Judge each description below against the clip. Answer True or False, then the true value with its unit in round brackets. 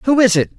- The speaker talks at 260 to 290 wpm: False (305 wpm)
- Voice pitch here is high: True (225 Hz)